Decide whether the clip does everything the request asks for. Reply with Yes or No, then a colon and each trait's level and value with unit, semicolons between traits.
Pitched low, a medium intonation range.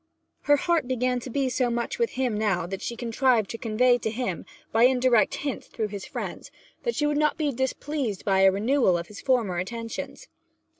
No: high, 240 Hz; average, 3.7 semitones